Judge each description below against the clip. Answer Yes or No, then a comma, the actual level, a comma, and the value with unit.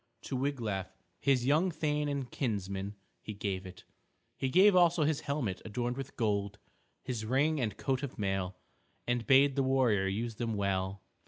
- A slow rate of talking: No, average, 165 wpm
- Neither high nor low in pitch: No, low, 120 Hz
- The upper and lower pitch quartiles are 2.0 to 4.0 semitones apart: No, wide, 5.6 semitones